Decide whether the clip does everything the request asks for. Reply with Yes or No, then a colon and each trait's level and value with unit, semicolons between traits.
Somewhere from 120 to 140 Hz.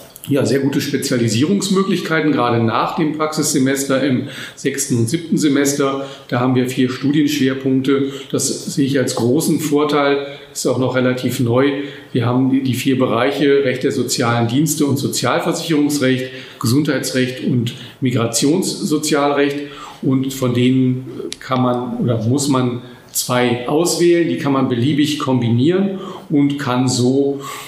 Yes: low, 135 Hz